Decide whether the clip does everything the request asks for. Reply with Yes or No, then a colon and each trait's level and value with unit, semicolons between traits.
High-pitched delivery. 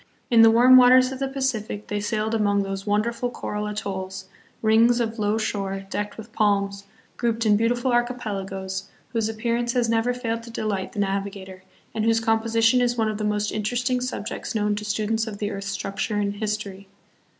Yes: high, 215 Hz